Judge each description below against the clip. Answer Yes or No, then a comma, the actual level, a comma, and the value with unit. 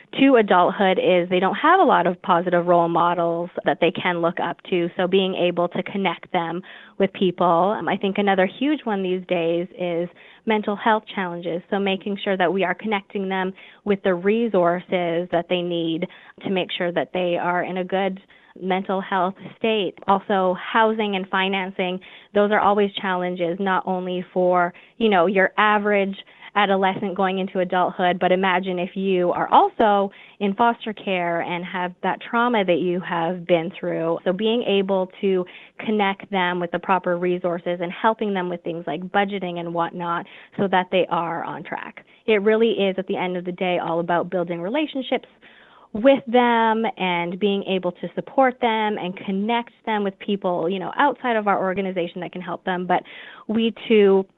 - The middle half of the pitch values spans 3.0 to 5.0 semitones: No, narrow, 2.4 semitones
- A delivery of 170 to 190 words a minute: Yes, average, 180 wpm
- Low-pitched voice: No, medium, 185 Hz